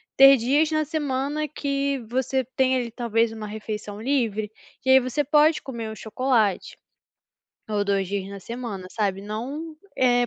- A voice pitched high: Yes, high, 245 Hz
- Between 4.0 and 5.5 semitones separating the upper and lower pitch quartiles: Yes, average, 4.3 semitones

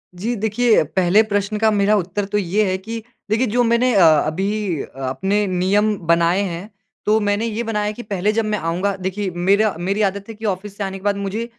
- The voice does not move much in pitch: Yes, narrow, 2.1 semitones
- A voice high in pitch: Yes, high, 205 Hz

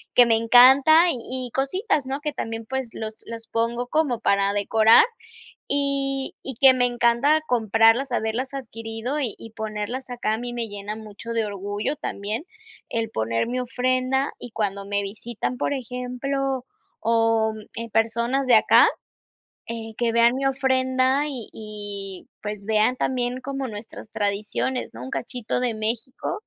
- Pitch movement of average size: Yes, average, 3.0 semitones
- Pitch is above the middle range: Yes, high, 235 Hz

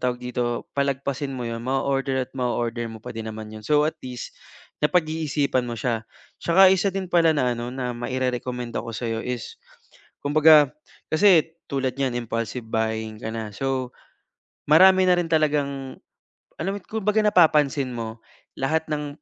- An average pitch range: Yes, average, 4.4 semitones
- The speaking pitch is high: No, low, 135 Hz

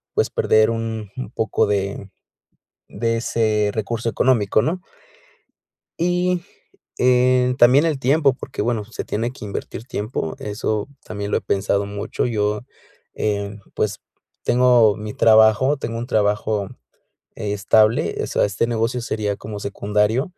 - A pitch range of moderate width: Yes, average, 3.1 semitones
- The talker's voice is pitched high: No, low, 110 Hz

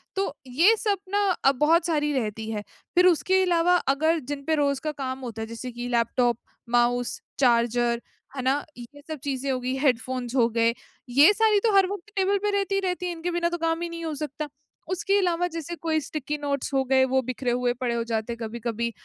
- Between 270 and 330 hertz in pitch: Yes, very high, 280 Hz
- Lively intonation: Yes, wide, 6.0 semitones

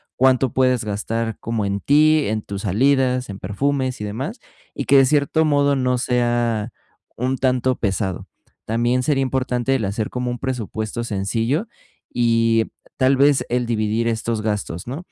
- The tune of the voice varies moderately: Yes, average, 3.2 semitones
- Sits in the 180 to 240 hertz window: No, low, 120 Hz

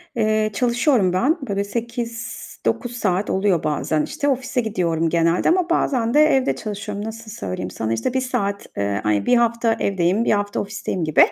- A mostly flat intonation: No, average, 5.1 semitones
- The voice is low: No, high, 215 Hz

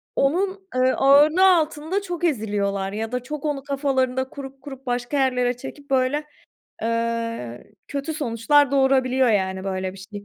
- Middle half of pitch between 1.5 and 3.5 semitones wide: No, average, 4.0 semitones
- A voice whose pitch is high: Yes, very high, 265 Hz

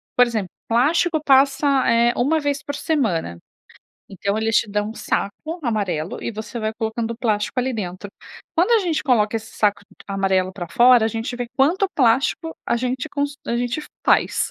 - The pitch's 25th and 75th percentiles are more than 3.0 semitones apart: Yes, average, 4.9 semitones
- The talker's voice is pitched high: Yes, high, 235 Hz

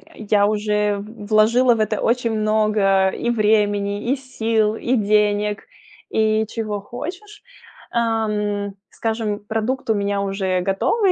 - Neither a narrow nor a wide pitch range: No, narrow, 1.8 semitones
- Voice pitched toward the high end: Yes, high, 215 Hz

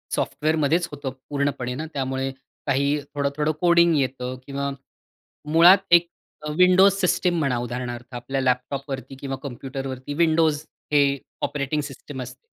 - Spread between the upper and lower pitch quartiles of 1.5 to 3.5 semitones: Yes, average, 2.9 semitones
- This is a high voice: No, medium, 140 Hz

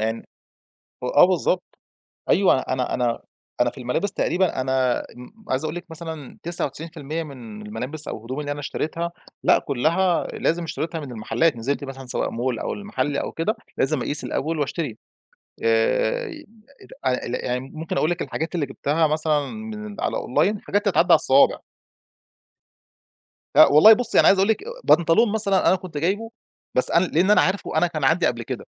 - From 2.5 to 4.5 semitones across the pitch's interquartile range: No, wide, 5.5 semitones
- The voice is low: No, medium, 155 Hz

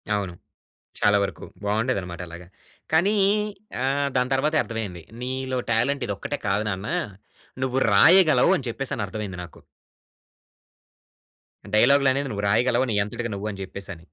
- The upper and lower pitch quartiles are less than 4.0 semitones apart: No, average, 5.0 semitones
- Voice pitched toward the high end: No, low, 115 Hz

